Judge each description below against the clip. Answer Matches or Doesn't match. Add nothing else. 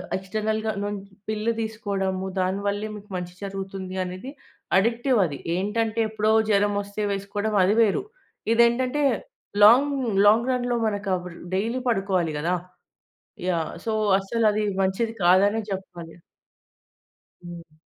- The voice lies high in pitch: Matches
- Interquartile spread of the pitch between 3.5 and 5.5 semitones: Doesn't match